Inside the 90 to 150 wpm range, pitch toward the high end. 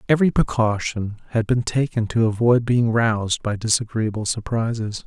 No: average, 140 wpm; low, 115 Hz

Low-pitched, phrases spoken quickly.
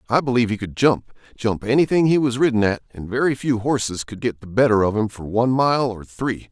Yes: low, 120 Hz; fast, 230 wpm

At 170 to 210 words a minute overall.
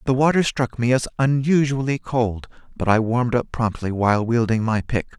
Yes: average, 185 wpm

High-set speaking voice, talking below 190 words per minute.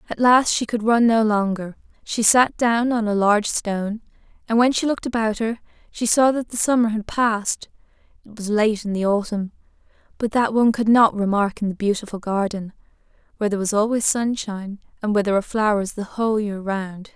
No: high, 215 Hz; average, 200 wpm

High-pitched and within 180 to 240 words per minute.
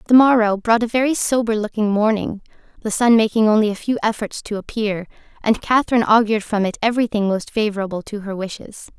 Yes: high, 215 Hz; average, 185 wpm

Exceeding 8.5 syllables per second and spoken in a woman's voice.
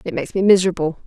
Yes: 8.7 syllables/s; female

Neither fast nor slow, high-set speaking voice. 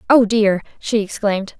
Yes: average, 150 wpm; high, 210 Hz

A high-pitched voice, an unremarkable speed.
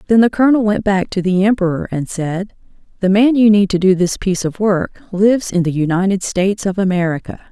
No: high, 195 Hz; fast, 215 wpm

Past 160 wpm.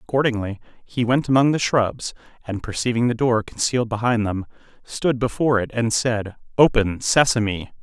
No: average, 155 wpm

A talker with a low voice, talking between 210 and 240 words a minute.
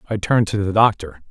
Yes: low, 100 Hz; fast, 230 wpm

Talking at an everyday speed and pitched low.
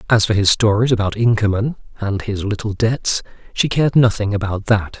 Yes: average, 180 wpm; low, 110 Hz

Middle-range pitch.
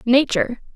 No: high, 235 Hz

